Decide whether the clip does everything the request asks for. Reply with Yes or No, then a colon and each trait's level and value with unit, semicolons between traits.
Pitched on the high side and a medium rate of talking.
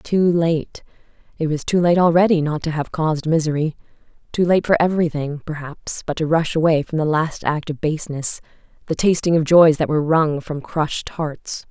No: medium, 160 Hz; average, 185 wpm